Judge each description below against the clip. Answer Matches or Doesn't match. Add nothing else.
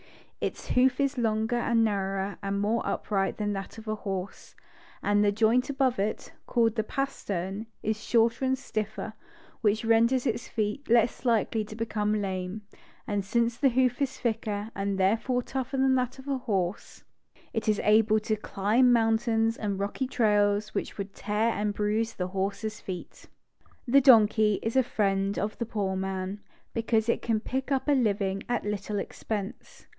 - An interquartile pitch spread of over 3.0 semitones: Doesn't match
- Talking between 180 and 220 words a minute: Doesn't match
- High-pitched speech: Matches